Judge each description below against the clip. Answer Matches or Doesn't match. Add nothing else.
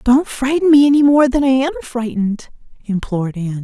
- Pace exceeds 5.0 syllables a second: Matches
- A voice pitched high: Matches